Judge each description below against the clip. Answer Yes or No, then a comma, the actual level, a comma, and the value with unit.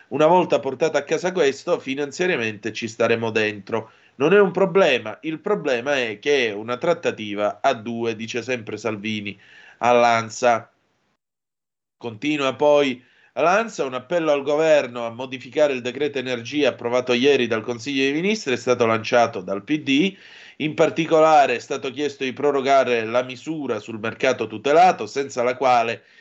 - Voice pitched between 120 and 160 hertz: Yes, low, 130 Hz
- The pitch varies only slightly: No, average, 4.4 semitones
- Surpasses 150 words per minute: No, average, 145 wpm